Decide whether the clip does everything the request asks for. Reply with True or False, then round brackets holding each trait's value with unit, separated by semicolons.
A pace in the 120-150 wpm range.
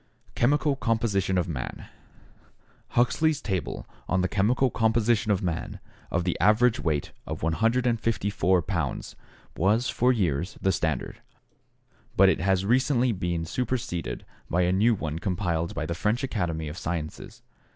True (140 wpm)